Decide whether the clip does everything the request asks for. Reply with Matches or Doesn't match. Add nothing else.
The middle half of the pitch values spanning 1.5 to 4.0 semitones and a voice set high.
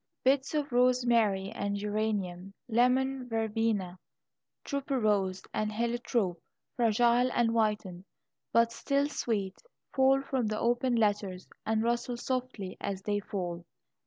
Matches